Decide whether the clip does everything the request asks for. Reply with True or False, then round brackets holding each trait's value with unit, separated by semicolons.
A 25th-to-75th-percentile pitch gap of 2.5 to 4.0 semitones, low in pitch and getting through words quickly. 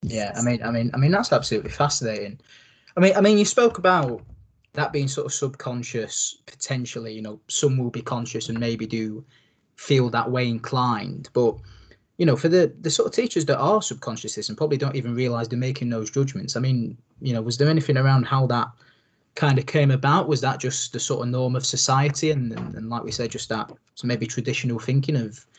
True (3.7 semitones; 125 Hz; 215 wpm)